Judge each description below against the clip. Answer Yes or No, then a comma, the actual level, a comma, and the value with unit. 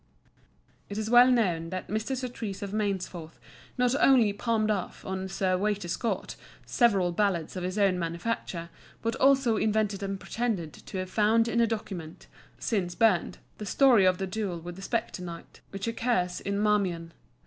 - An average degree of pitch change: Yes, average, 3.8 semitones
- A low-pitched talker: No, high, 200 Hz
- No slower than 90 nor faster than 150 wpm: No, average, 170 wpm